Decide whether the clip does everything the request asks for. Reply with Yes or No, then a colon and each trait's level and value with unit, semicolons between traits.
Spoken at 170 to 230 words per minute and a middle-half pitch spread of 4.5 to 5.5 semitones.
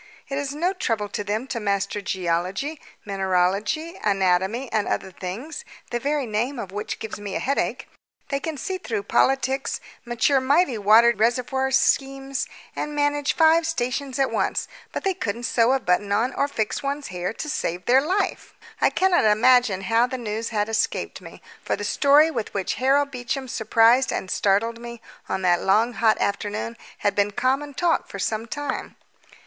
Yes: average, 175 wpm; average, 5.2 semitones